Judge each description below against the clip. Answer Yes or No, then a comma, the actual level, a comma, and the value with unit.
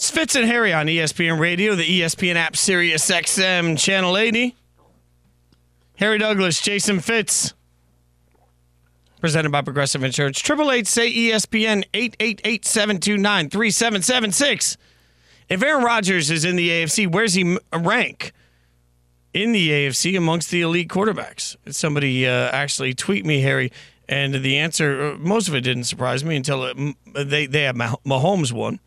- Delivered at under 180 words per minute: Yes, slow, 135 wpm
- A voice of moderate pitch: Yes, medium, 165 Hz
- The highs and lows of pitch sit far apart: Yes, wide, 7.6 semitones